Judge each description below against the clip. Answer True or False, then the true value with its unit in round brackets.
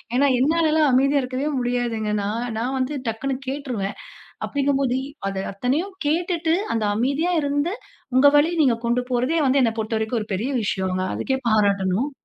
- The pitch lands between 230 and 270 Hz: True (255 Hz)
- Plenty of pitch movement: False (4.3 semitones)